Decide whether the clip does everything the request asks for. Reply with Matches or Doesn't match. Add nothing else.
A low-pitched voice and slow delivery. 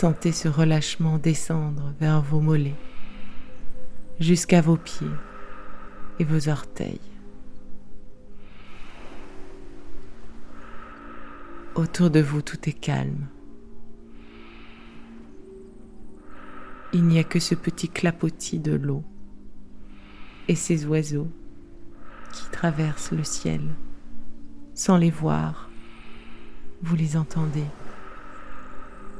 Doesn't match